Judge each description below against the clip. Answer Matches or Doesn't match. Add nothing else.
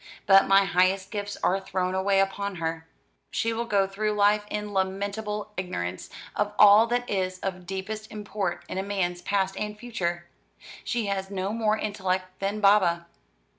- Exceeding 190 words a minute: Doesn't match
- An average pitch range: Doesn't match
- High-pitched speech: Matches